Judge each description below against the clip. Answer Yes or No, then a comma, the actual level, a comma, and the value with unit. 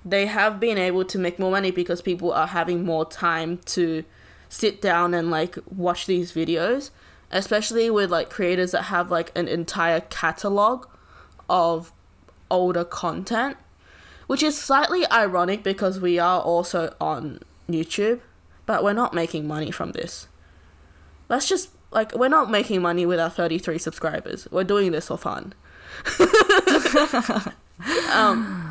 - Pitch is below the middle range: No, medium, 180 Hz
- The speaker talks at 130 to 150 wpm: Yes, average, 145 wpm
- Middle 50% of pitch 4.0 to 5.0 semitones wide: Yes, average, 4.3 semitones